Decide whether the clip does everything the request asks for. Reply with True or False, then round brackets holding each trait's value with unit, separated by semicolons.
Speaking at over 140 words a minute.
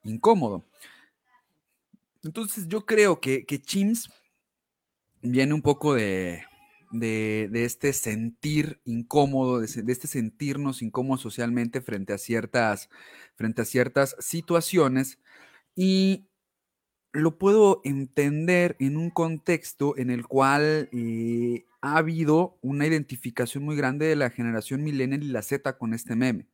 False (125 wpm)